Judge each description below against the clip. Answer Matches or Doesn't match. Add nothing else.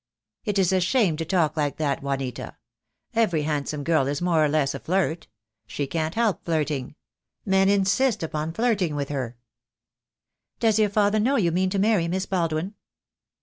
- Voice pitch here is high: Doesn't match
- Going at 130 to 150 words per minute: Doesn't match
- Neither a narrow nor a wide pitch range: Matches